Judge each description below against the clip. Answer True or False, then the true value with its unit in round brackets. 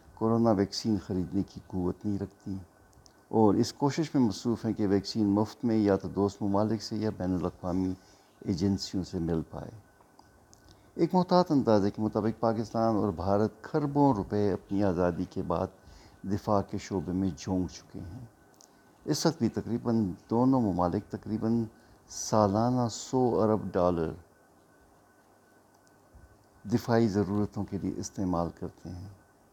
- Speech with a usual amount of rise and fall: True (3.1 semitones)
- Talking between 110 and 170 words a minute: True (140 wpm)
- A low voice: True (100 Hz)